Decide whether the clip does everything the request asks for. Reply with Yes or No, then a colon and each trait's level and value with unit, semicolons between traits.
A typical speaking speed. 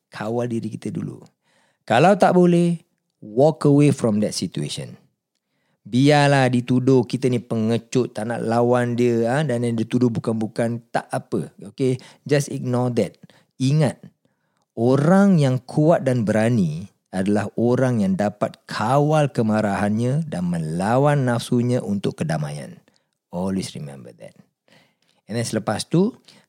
Yes: average, 125 wpm